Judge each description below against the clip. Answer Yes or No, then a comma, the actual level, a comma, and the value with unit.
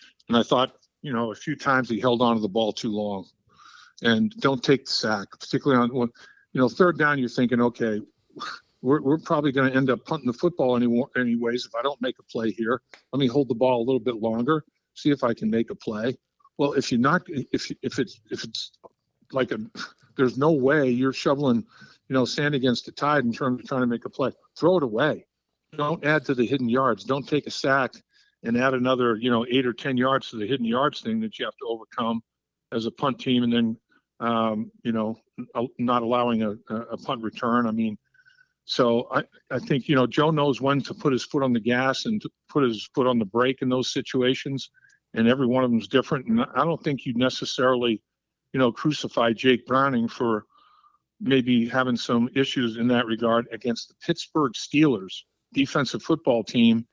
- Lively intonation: No, average, 3.2 semitones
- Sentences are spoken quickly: Yes, fast, 215 wpm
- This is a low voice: Yes, low, 125 Hz